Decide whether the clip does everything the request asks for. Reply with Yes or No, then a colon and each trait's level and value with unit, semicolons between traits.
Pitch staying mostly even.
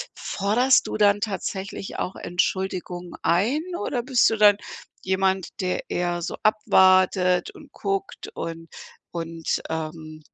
No: average, 3.2 semitones